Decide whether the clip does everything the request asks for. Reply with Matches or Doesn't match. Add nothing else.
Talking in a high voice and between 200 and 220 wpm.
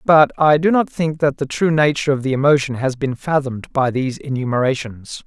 Doesn't match